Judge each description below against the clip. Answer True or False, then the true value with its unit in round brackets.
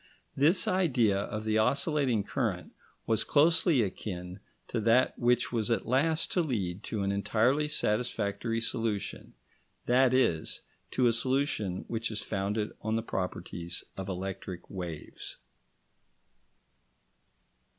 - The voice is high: False (115 Hz)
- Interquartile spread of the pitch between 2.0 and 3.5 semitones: False (4.7 semitones)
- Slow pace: True (120 wpm)